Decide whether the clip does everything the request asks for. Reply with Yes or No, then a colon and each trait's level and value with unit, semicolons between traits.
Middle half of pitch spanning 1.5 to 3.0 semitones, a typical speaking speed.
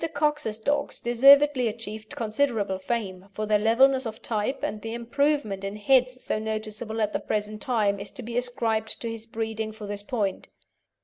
Yes: average, 2.7 semitones; average, 175 wpm